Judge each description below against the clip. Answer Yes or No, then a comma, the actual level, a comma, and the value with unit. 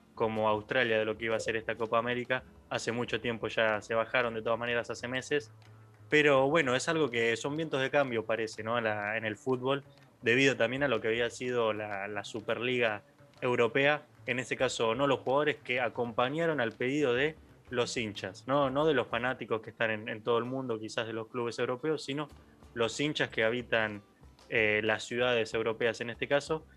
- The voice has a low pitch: Yes, low, 120 Hz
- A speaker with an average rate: No, fast, 200 wpm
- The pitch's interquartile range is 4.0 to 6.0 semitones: No, average, 3.5 semitones